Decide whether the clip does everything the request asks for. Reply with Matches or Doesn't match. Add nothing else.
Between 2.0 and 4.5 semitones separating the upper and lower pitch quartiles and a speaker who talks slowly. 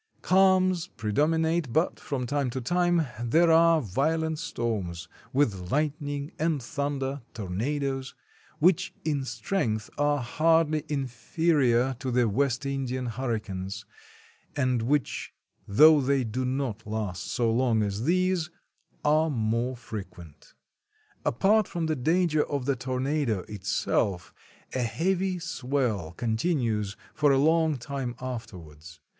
Doesn't match